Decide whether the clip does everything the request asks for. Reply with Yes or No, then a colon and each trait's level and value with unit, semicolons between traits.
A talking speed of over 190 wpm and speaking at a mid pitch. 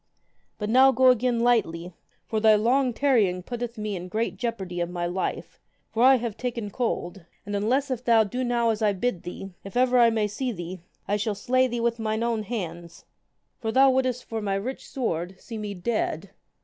No: average, 200 wpm; high, 225 Hz